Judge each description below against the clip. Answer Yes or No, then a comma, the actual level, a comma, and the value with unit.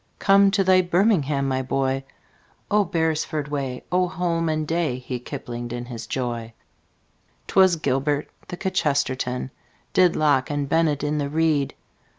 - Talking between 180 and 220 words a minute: No, average, 140 wpm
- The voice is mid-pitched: Yes, medium, 145 Hz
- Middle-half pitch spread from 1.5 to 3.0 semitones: No, average, 4.5 semitones